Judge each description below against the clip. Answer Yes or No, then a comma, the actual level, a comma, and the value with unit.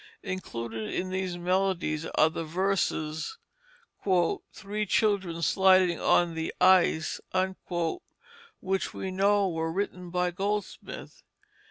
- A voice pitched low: No, medium, 185 Hz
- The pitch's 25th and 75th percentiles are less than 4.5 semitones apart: Yes, average, 2.7 semitones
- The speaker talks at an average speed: No, slow, 105 wpm